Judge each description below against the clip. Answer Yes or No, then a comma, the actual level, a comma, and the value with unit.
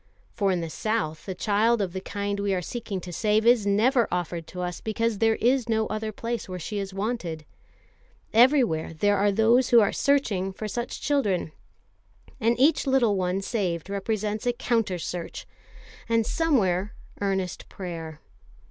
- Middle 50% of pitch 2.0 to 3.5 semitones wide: No, average, 3.9 semitones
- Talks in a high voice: Yes, high, 205 Hz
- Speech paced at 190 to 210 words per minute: No, average, 165 wpm